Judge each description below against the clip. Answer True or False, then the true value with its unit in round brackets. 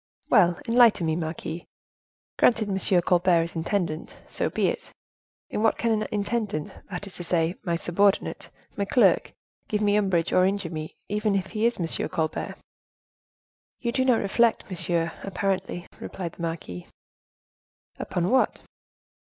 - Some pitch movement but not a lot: True (3.8 semitones)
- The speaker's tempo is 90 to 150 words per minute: True (145 wpm)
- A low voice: False (190 Hz)